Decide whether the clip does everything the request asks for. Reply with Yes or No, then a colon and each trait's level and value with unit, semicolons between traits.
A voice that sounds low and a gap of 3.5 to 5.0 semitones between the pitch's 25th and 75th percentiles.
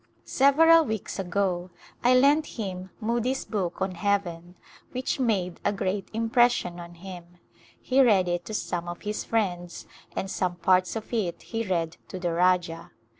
No: high, 190 Hz; average, 4.4 semitones